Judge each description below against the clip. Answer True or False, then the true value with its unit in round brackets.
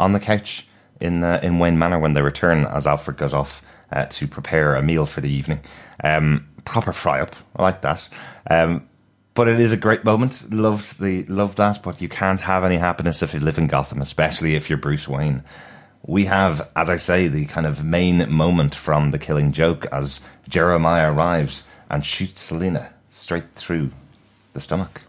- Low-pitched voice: True (80 Hz)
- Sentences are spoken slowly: False (190 wpm)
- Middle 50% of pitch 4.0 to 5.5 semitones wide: True (4.3 semitones)